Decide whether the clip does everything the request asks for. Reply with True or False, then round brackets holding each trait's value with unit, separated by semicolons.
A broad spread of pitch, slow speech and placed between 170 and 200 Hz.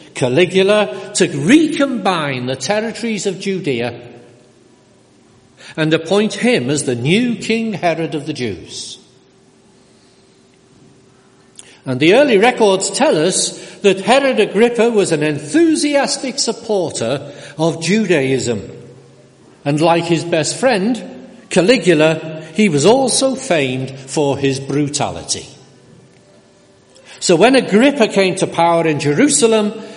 True (7.1 semitones; 110 wpm; 185 Hz)